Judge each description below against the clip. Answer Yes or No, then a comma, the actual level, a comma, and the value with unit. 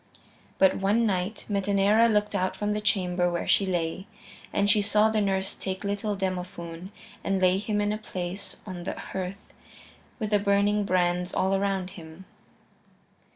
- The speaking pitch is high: Yes, high, 195 Hz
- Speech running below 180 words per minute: Yes, average, 160 wpm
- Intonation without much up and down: Yes, narrow, 2.1 semitones